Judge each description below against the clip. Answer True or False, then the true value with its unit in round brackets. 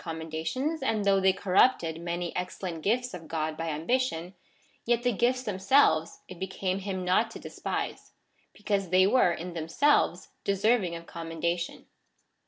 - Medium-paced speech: True (150 wpm)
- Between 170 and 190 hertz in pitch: True (185 Hz)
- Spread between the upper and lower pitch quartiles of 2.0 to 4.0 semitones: False (4.8 semitones)